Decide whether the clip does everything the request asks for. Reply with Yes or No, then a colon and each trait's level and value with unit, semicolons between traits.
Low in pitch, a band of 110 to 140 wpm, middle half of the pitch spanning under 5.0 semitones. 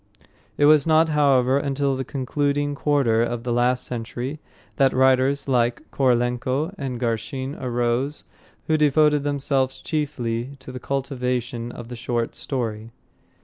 Yes: low, 130 Hz; slow, 135 wpm; average, 2.8 semitones